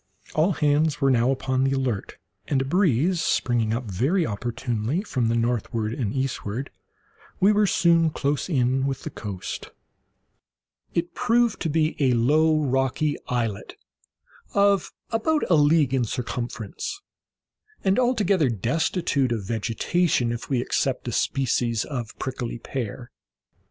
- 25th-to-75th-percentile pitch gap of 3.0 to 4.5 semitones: No, wide, 5.4 semitones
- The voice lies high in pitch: No, low, 135 Hz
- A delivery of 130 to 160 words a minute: Yes, slow, 135 wpm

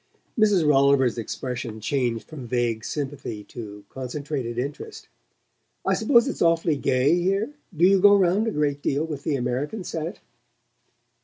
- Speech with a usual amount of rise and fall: No, wide, 5.9 semitones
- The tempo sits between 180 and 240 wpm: No, average, 145 wpm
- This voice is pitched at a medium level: Yes, medium, 145 Hz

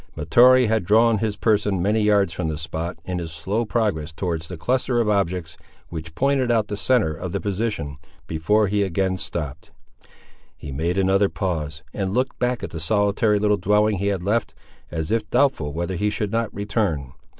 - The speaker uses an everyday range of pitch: Yes, average, 4.7 semitones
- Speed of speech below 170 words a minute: No, average, 185 wpm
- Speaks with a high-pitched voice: No, low, 100 Hz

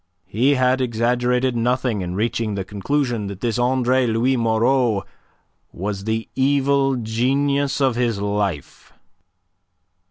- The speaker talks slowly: Yes, slow, 120 wpm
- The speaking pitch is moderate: No, low, 120 Hz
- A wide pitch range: No, average, 3.2 semitones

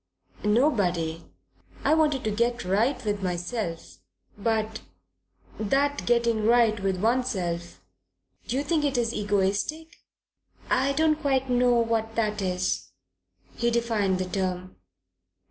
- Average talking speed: No, slow, 115 wpm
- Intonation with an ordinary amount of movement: Yes, average, 4.9 semitones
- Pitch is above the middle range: Yes, high, 225 Hz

